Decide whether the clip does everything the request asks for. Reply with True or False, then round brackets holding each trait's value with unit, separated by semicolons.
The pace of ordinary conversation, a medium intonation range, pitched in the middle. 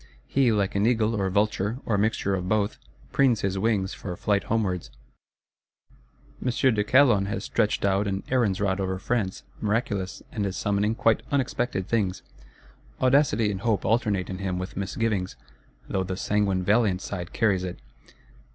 False (160 wpm; 3.0 semitones; 100 Hz)